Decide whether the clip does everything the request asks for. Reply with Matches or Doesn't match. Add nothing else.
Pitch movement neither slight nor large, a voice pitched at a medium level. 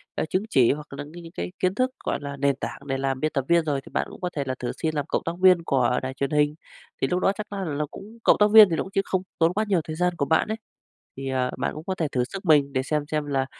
Matches